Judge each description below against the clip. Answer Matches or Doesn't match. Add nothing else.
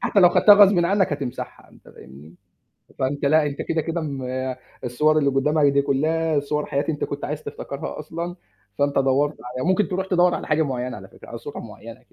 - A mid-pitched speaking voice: Matches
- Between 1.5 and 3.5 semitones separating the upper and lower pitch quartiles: Matches